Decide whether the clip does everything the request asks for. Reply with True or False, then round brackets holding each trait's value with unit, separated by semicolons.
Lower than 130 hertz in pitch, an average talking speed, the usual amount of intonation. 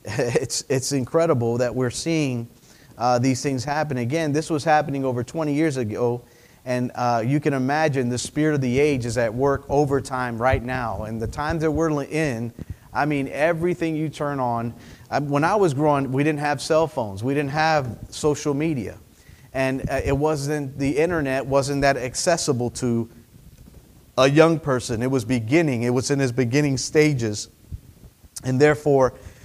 False (135 Hz; 175 wpm; 3.5 semitones)